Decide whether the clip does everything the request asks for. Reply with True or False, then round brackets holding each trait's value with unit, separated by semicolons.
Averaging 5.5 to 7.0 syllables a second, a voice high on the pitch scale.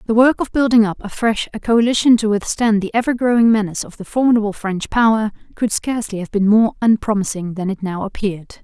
True (6.2 syllables/s; 215 Hz)